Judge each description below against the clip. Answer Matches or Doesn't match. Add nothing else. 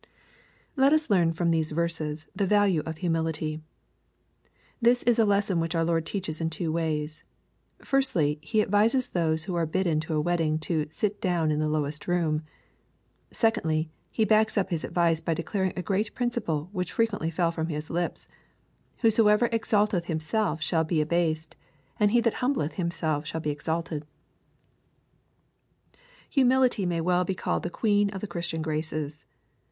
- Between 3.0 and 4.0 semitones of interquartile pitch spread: Doesn't match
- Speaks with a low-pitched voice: Doesn't match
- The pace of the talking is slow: Doesn't match